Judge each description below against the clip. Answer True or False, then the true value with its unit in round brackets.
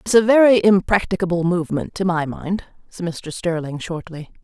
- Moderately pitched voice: True (180 Hz)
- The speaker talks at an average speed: True (160 wpm)